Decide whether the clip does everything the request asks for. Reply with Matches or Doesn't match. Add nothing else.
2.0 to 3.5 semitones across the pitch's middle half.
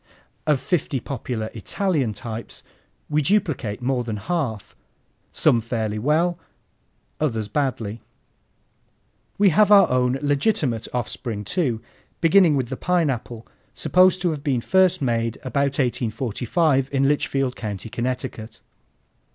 Doesn't match